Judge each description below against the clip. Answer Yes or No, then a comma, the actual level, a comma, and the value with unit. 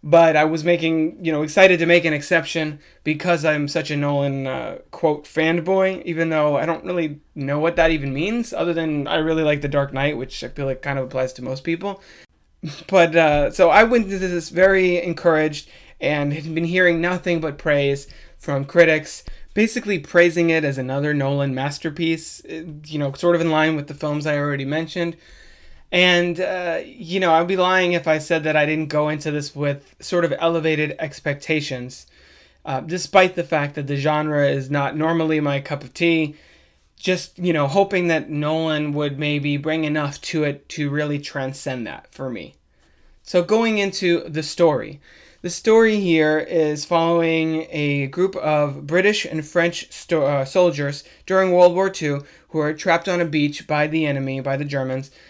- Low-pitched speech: No, medium, 155 Hz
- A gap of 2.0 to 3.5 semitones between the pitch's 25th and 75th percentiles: Yes, average, 2.9 semitones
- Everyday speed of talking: Yes, average, 185 wpm